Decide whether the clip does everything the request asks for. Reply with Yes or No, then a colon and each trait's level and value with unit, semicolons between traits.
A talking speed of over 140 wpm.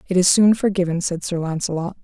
Yes: fast, 205 wpm